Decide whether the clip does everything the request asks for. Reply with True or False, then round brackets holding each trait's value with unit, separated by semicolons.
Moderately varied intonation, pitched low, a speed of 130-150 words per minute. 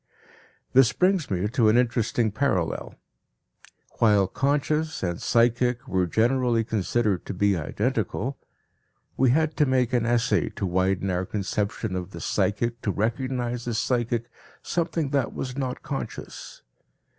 True (4.4 semitones; 120 Hz; 135 wpm)